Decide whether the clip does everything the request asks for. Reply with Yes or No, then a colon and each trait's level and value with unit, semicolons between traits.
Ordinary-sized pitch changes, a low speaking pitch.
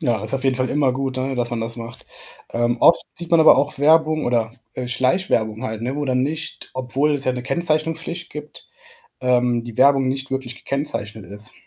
Yes: average, 3.5 semitones; low, 130 Hz